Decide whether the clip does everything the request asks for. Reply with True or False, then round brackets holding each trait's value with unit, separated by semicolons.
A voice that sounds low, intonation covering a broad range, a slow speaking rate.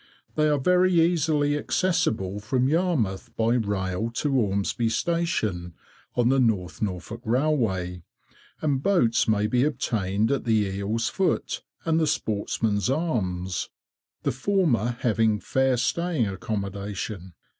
True (115 Hz; 6.6 semitones; 125 wpm)